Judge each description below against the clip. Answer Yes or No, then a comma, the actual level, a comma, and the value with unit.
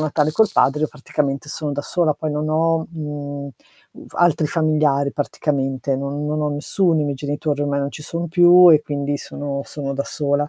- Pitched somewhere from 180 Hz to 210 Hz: No, medium, 145 Hz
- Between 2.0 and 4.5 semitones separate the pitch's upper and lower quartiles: No, narrow, 1.6 semitones